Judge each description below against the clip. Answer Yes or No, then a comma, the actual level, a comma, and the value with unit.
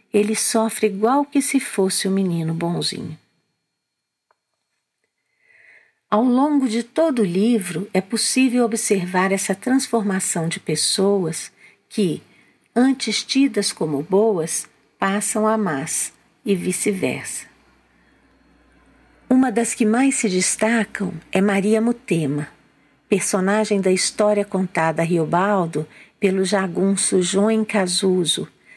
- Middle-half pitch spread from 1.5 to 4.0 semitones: Yes, average, 3.4 semitones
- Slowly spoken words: Yes, slow, 110 wpm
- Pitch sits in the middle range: No, high, 205 Hz